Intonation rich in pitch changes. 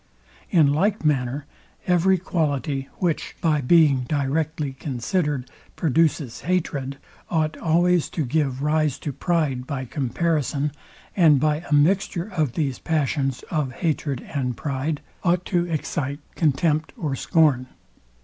No: average, 3.3 semitones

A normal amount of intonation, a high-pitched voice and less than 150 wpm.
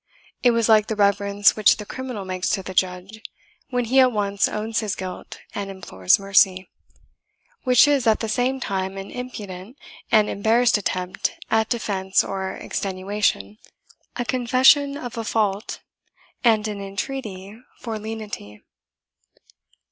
Yes: average, 3.4 semitones; high, 210 Hz; average, 140 wpm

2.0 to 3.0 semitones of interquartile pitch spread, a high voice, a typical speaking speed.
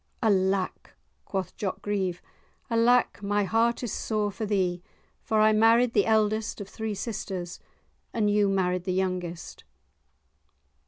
No: average, 2.7 semitones; high, 205 Hz; slow, 130 wpm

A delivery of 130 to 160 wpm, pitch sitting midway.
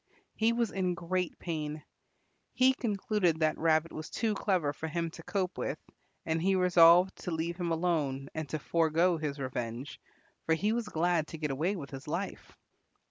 No: average, 180 wpm; medium, 165 Hz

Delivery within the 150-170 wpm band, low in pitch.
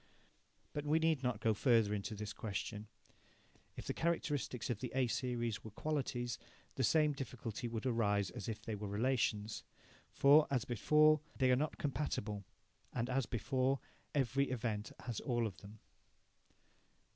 Yes: average, 155 wpm; low, 120 Hz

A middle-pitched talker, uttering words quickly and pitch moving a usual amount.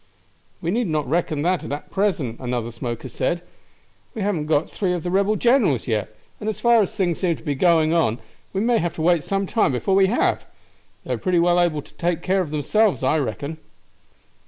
Yes: medium, 175 Hz; fast, 215 wpm; average, 5.0 semitones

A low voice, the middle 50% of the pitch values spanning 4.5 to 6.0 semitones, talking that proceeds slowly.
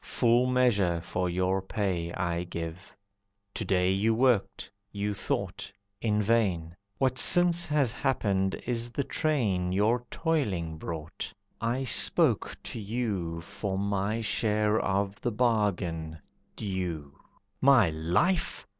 Yes: low, 100 Hz; average, 4.9 semitones; slow, 120 wpm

